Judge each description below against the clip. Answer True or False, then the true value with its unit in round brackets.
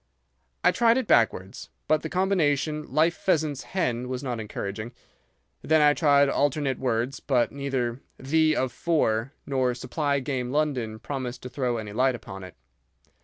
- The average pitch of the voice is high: False (135 Hz)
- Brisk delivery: False (155 wpm)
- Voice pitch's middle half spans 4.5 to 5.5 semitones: False (4.0 semitones)